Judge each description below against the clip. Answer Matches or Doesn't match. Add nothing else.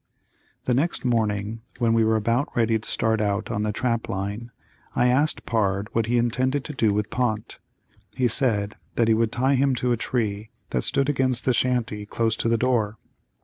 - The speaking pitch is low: Matches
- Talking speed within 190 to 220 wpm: Matches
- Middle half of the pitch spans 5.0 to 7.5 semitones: Doesn't match